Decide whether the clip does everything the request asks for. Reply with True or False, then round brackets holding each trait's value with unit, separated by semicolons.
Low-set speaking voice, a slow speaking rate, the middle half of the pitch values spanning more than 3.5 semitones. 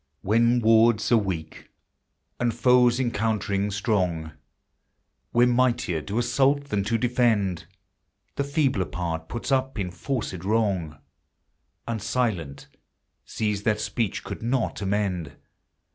True (110 Hz; 115 wpm; 4.2 semitones)